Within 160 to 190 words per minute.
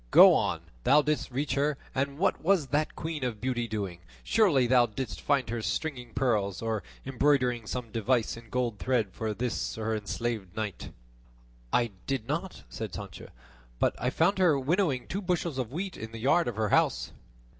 Yes: average, 180 wpm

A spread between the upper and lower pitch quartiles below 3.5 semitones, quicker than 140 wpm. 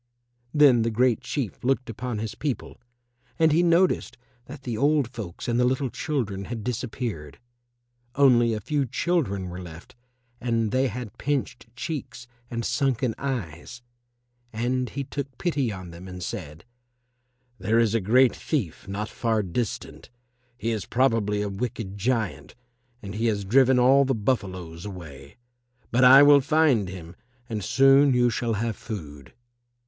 No: average, 4.7 semitones; average, 155 wpm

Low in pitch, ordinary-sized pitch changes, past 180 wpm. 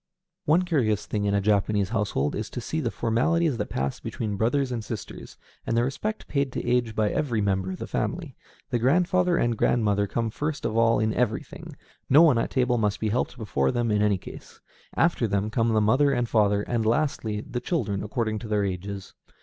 Yes: low, 115 Hz; average, 3.3 semitones; fast, 205 wpm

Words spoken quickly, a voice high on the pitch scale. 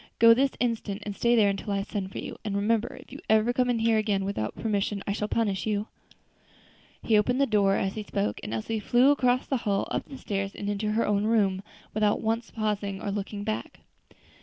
Yes: fast, 220 wpm; high, 210 Hz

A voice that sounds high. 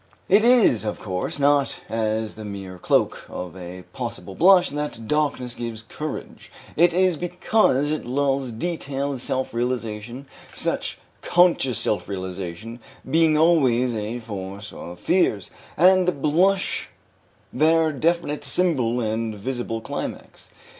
No: low, 130 Hz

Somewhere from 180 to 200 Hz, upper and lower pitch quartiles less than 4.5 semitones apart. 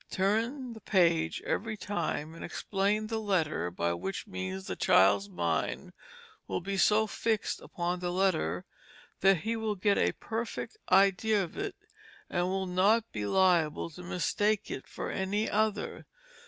No: high, 190 Hz; average, 4.8 semitones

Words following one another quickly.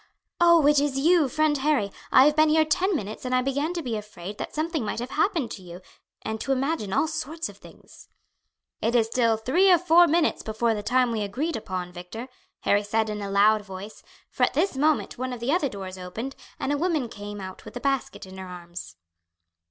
Yes: fast, 220 wpm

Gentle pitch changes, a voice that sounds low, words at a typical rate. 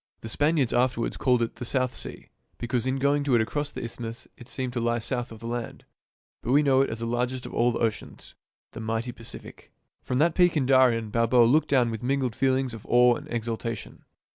No: narrow, 2.2 semitones; low, 120 Hz; fast, 225 wpm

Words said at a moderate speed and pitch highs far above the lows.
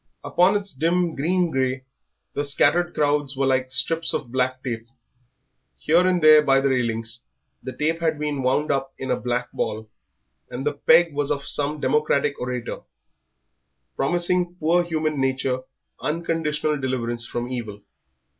No: average, 145 wpm; average, 4.0 semitones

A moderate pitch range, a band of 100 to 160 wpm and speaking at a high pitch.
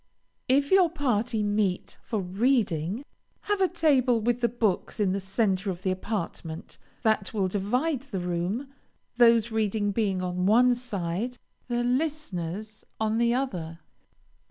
Yes: average, 4.7 semitones; average, 140 wpm; high, 220 Hz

